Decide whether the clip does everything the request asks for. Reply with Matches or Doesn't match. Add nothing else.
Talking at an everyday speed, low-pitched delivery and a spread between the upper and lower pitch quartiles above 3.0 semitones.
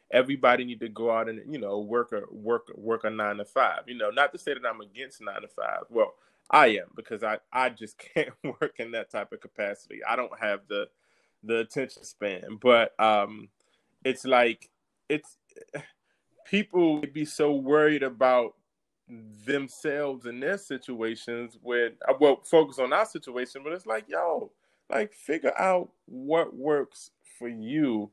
Matches